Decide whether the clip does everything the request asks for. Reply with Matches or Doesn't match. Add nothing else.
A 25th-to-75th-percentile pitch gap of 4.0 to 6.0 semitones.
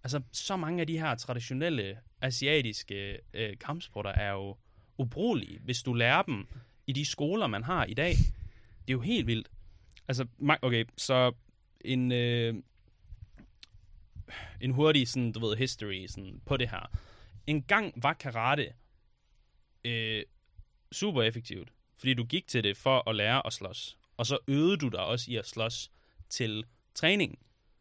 Matches